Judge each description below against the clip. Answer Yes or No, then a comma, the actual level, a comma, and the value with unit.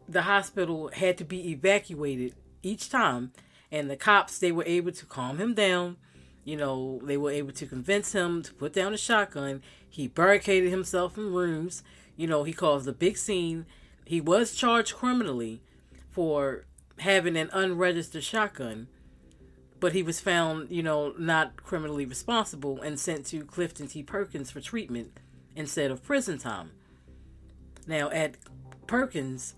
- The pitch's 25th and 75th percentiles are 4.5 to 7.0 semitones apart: Yes, wide, 5.5 semitones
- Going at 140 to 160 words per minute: Yes, average, 155 wpm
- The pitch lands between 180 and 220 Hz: No, medium, 160 Hz